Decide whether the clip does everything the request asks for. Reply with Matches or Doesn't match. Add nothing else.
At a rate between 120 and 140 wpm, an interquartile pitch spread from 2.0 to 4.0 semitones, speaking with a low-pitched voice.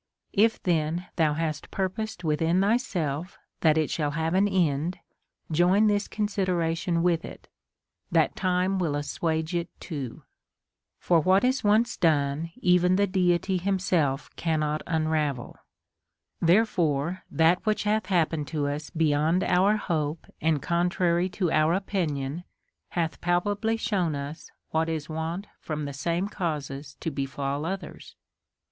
Doesn't match